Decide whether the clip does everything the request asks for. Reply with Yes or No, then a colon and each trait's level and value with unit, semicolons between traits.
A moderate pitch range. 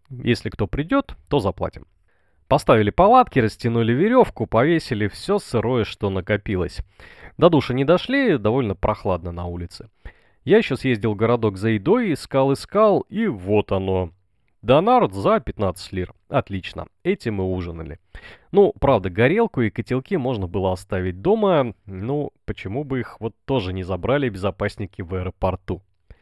No: wide, 6.3 semitones